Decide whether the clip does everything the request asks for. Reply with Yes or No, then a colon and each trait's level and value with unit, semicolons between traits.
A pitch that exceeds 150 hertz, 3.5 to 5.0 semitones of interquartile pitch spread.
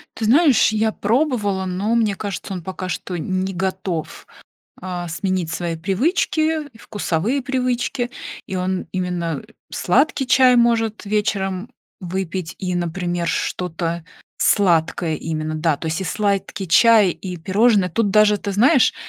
Yes: high, 190 Hz; average, 4.2 semitones